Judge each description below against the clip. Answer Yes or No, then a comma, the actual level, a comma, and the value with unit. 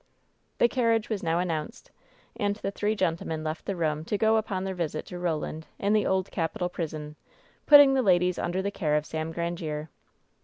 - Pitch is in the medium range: Yes, medium, 180 Hz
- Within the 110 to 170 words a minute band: No, average, 195 wpm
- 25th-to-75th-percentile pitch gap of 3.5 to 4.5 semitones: Yes, average, 4.2 semitones